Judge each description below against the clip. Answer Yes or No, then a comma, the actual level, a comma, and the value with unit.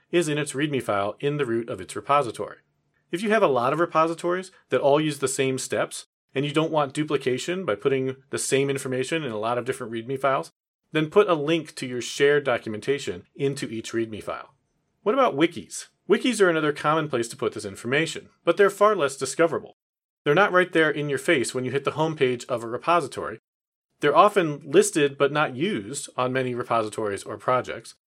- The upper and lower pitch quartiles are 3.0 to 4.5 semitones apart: Yes, average, 3.8 semitones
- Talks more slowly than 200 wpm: No, fast, 205 wpm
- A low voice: No, medium, 145 Hz